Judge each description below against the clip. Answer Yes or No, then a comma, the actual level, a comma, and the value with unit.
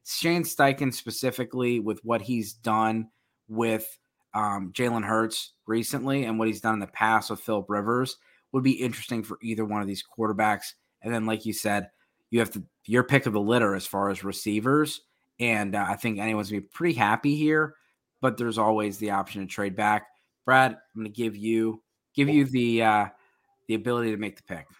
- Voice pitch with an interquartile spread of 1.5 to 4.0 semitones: Yes, average, 2.9 semitones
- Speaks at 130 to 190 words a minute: No, average, 200 wpm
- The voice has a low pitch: Yes, low, 110 Hz